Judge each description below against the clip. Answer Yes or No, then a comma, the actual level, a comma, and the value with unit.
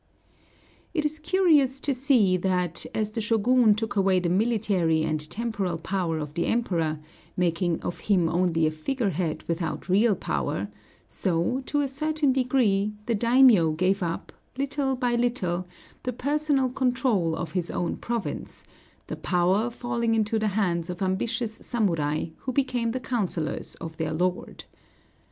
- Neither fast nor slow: Yes, average, 150 wpm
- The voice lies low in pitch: No, high, 205 Hz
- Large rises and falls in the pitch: Yes, wide, 6.1 semitones